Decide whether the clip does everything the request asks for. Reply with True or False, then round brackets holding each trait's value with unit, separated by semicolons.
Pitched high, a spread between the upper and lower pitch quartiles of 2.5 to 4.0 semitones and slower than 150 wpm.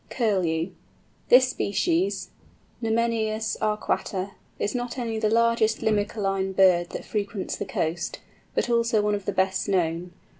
True (210 Hz; 3.3 semitones; 135 wpm)